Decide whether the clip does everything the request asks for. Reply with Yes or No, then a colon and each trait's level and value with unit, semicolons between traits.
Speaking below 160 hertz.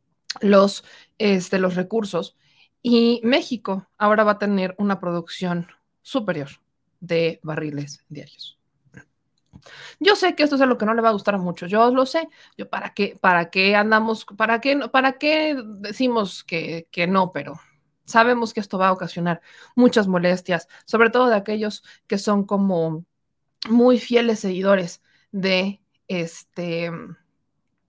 No: high, 195 Hz